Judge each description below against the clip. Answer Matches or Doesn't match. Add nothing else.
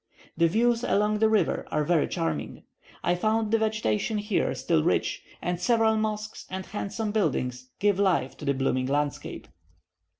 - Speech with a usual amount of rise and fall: Doesn't match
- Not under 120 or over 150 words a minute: Doesn't match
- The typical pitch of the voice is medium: Doesn't match